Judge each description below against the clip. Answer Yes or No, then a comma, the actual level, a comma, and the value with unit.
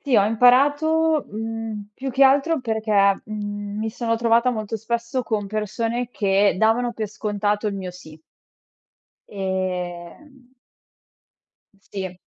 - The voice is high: Yes, high, 220 Hz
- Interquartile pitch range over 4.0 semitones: No, average, 3.2 semitones